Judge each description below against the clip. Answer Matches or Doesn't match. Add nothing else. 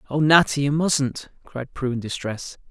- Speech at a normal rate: Matches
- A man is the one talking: Matches